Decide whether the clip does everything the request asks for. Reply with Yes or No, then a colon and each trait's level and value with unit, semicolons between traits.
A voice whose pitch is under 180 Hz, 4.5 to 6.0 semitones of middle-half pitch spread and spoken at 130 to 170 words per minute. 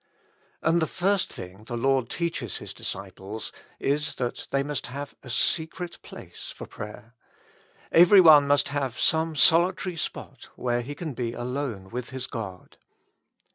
Yes: medium, 140 Hz; average, 5.2 semitones; average, 150 wpm